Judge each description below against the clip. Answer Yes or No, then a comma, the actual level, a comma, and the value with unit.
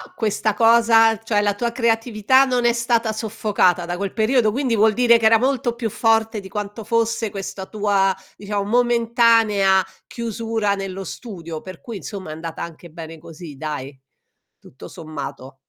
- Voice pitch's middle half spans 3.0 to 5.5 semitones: Yes, average, 3.3 semitones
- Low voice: No, high, 215 Hz